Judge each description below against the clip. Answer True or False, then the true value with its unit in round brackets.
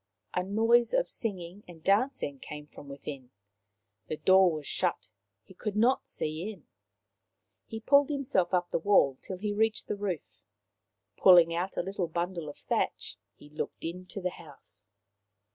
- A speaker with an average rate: True (160 wpm)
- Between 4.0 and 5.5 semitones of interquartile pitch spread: True (4.8 semitones)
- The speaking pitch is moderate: True (180 Hz)